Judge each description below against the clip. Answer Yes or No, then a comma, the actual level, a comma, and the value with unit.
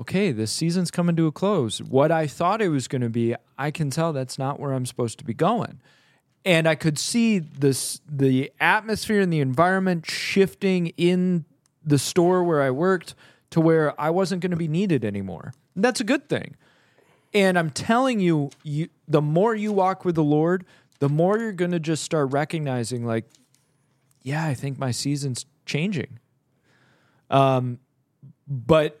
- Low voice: No, medium, 150 Hz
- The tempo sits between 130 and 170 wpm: No, average, 180 wpm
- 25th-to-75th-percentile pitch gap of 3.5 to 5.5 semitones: Yes, average, 4.8 semitones